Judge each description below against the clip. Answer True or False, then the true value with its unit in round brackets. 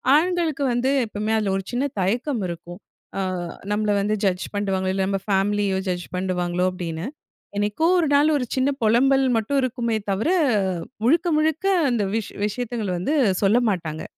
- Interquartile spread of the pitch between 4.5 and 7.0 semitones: True (5.4 semitones)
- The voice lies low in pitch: False (215 Hz)